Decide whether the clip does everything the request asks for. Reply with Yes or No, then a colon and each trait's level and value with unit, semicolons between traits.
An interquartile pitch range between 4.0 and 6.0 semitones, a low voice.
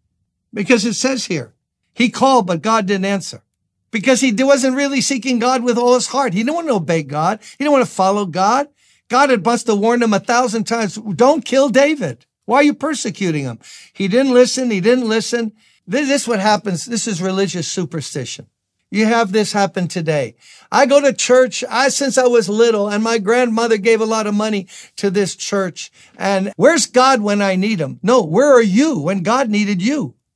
No: average, 4.7 semitones; high, 225 Hz